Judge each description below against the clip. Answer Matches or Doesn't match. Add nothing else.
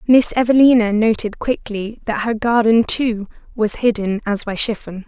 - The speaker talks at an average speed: Matches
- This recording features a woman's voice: Matches